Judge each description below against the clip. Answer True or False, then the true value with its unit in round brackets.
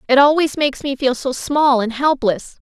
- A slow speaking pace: False (205 wpm)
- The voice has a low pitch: False (270 Hz)